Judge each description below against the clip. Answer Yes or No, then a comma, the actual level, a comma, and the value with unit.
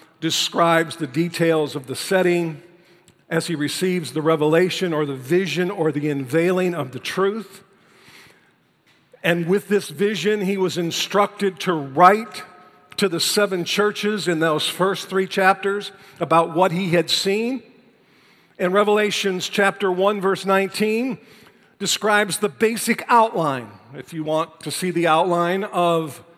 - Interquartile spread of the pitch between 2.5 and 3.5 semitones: Yes, average, 3.2 semitones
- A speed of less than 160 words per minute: Yes, average, 140 wpm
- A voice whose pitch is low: No, medium, 180 Hz